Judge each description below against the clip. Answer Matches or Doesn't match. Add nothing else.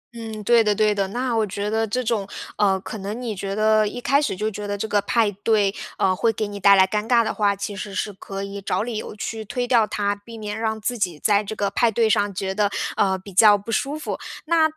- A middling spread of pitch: Doesn't match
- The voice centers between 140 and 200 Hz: Doesn't match